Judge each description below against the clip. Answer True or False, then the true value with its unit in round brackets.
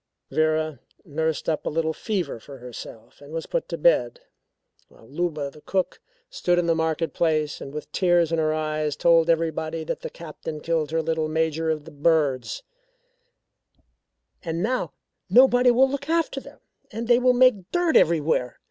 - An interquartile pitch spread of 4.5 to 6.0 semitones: False (2.9 semitones)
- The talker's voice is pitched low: False (160 Hz)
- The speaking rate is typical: True (170 wpm)